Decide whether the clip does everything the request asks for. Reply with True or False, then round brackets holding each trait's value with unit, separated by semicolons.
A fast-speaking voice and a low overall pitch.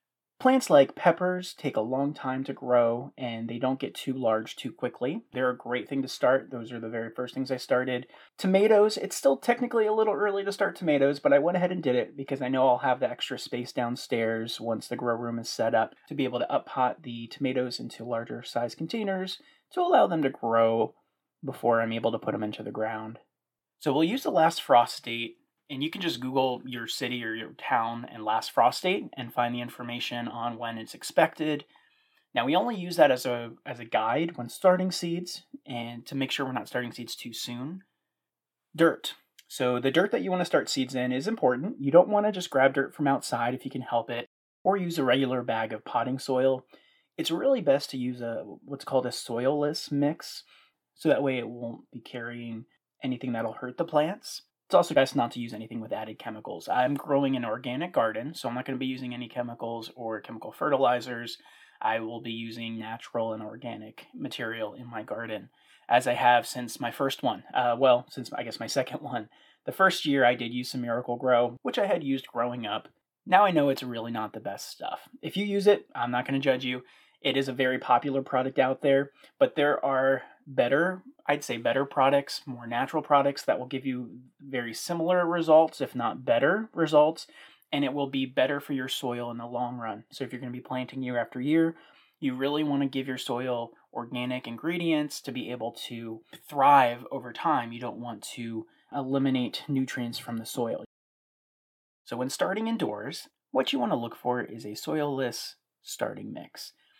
True (210 wpm; 130 Hz)